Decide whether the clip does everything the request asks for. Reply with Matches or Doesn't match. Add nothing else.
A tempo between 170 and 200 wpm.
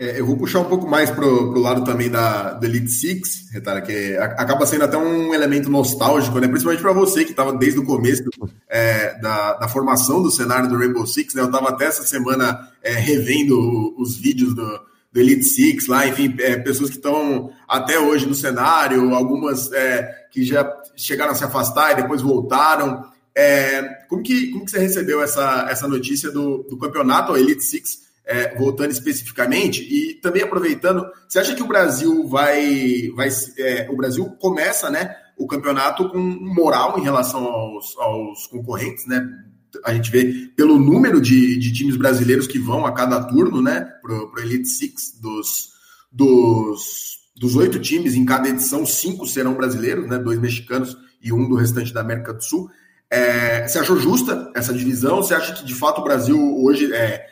Matches